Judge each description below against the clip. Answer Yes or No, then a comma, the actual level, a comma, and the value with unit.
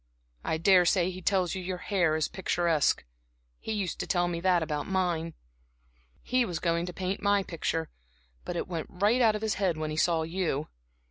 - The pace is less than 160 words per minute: No, average, 185 wpm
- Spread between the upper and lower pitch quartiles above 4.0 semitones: No, narrow, 2.5 semitones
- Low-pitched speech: No, medium, 175 Hz